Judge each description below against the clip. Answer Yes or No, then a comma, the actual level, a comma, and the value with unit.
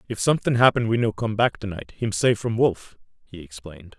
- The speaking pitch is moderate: No, low, 110 Hz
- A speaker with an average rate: No, fast, 225 wpm